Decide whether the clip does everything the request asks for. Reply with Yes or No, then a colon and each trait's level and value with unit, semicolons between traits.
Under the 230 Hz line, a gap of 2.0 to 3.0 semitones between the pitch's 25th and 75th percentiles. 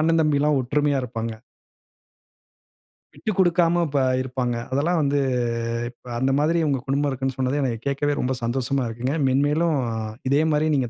Yes: medium, 140 Hz; narrow, 2.6 semitones